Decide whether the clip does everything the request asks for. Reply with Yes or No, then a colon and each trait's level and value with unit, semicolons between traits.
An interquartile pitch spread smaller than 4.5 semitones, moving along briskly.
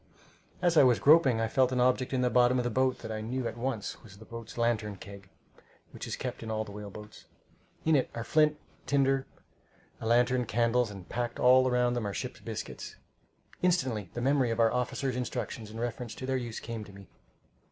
Yes: average, 2.7 semitones; fast, 210 wpm